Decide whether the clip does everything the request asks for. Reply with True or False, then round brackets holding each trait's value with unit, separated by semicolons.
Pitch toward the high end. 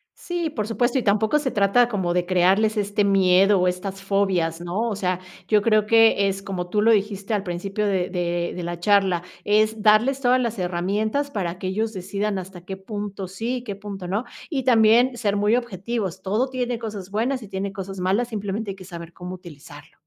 True (200 Hz)